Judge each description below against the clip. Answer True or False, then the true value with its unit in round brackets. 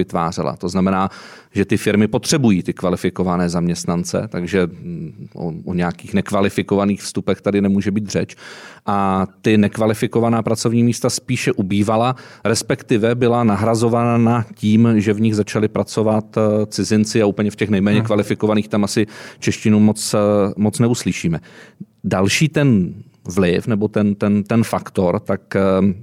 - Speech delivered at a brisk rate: False (135 wpm)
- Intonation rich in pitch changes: False (2.5 semitones)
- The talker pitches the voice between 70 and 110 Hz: True (105 Hz)